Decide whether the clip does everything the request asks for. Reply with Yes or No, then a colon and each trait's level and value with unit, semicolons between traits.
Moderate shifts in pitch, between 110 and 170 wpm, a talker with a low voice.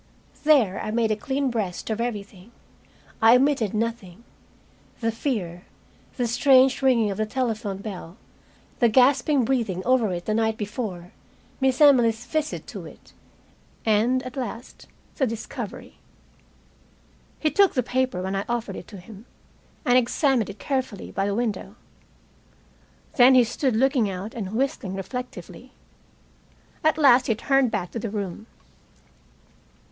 No: average, 4.0 semitones; average, 140 wpm; high, 230 Hz